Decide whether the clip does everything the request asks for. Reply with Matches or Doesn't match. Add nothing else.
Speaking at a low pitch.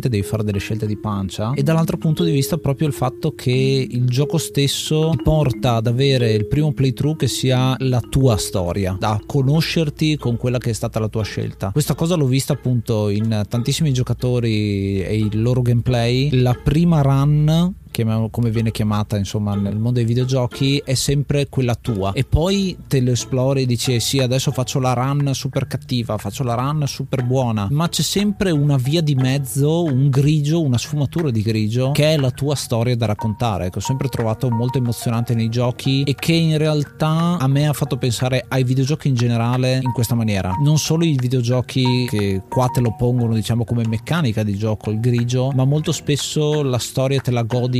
Matches